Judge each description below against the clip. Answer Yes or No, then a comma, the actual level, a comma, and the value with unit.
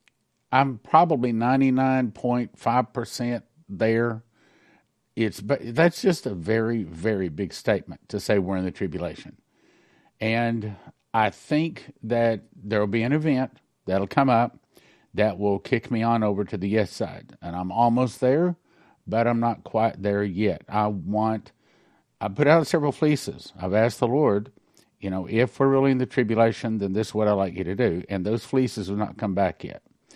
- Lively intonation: No, average, 3.6 semitones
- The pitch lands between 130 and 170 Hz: No, low, 115 Hz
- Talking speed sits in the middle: Yes, average, 175 wpm